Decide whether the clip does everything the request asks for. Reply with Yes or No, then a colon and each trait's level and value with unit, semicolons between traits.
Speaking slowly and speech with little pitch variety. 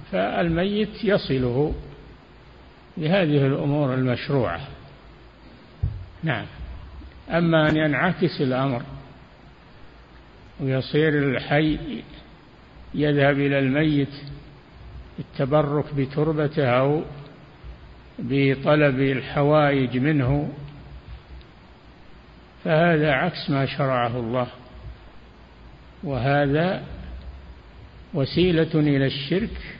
No: slow, 60 wpm; average, 3.1 semitones